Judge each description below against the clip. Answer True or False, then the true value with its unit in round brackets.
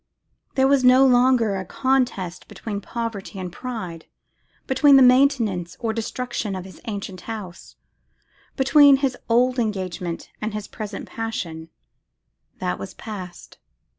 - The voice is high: True (225 Hz)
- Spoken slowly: True (130 wpm)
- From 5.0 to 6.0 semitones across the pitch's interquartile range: True (5.3 semitones)